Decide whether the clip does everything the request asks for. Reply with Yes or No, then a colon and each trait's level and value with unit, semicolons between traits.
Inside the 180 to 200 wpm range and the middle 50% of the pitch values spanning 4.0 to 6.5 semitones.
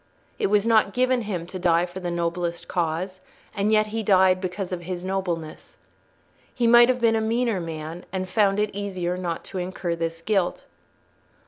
No: average, 185 wpm; average, 3.4 semitones